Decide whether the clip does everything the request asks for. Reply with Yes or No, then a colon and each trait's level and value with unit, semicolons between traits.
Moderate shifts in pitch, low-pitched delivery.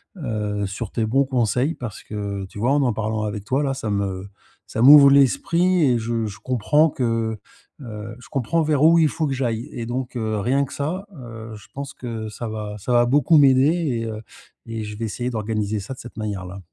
Yes: average, 4.1 semitones; low, 115 Hz